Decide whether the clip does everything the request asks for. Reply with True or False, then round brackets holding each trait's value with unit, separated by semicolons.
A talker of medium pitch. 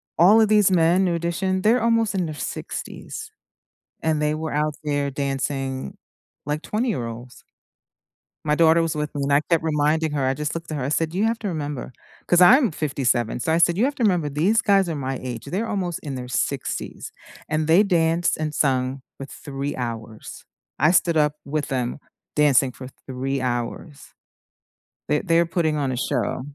True (155 Hz)